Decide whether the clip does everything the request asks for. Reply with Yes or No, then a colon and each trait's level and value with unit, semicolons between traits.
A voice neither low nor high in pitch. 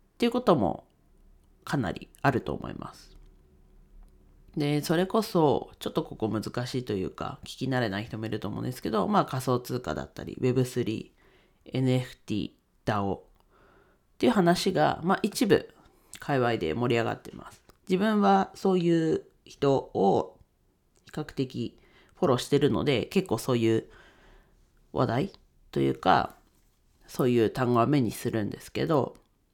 No: low, 125 Hz